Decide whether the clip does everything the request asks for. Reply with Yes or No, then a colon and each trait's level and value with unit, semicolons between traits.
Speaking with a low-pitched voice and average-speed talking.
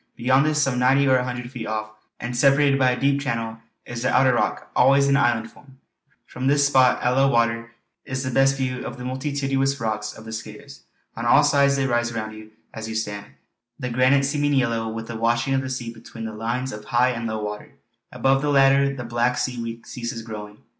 No: low, 125 Hz; fast, 220 wpm